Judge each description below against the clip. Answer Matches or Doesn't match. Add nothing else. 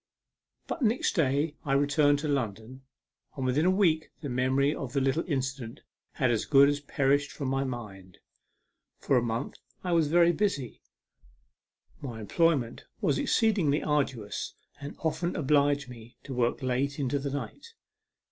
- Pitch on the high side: Doesn't match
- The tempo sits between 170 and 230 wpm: Doesn't match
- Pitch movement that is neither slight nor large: Matches